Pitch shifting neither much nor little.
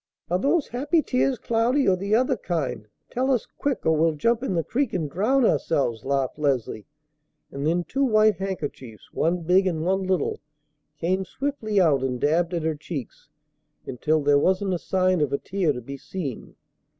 No: wide, 6.8 semitones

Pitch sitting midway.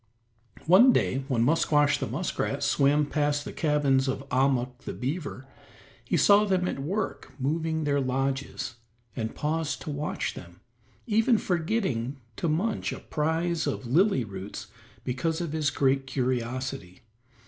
Yes: medium, 145 Hz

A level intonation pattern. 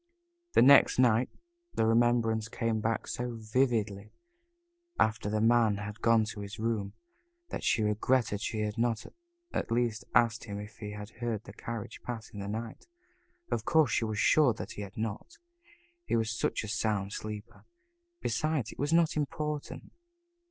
Yes: narrow, 2.1 semitones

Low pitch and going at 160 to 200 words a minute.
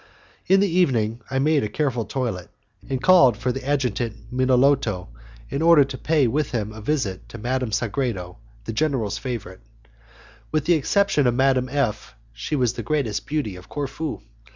Yes: low, 130 Hz; average, 170 wpm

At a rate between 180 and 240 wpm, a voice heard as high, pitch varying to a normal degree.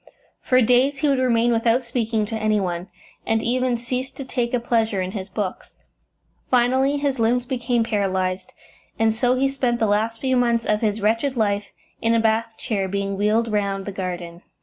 Yes: average, 190 wpm; high, 230 Hz; average, 3.2 semitones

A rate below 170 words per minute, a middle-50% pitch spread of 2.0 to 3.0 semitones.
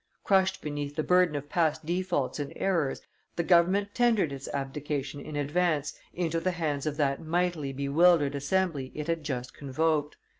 No: average, 160 wpm; average, 3.6 semitones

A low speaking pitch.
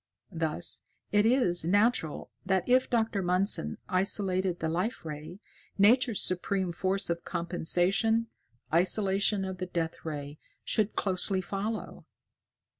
No: medium, 185 Hz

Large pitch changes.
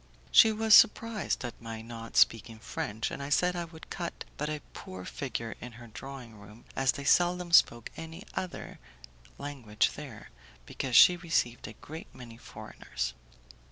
Yes: wide, 6.9 semitones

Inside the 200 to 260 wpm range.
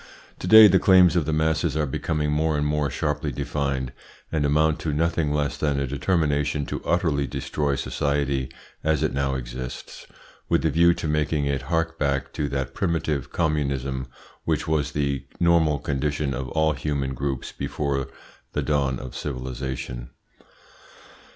No: average, 155 wpm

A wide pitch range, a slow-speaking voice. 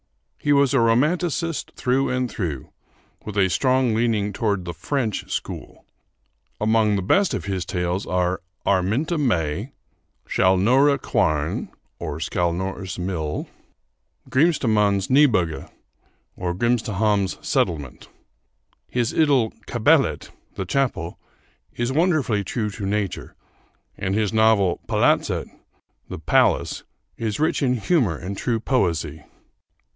Yes: wide, 5.7 semitones; slow, 110 wpm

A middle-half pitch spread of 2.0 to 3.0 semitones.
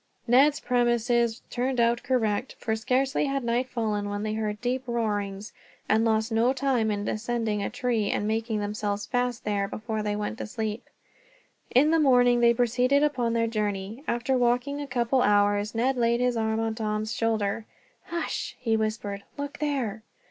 Yes: narrow, 2.6 semitones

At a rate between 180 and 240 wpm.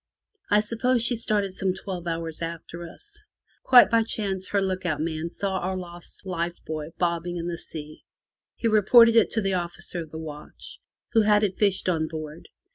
Yes: average, 190 wpm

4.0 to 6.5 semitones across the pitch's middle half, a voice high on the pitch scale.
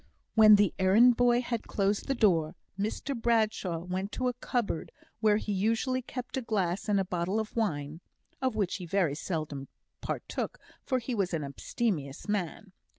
Yes: average, 4.7 semitones; high, 205 Hz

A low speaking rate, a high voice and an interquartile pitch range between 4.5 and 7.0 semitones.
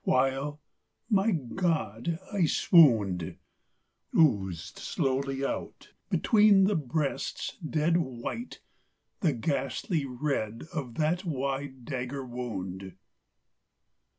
No: slow, 90 wpm; medium, 140 Hz; average, 5.0 semitones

